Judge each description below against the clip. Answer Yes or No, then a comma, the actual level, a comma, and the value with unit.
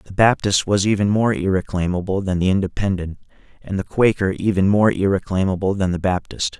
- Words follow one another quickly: No, average, 165 wpm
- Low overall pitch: Yes, very low, 95 Hz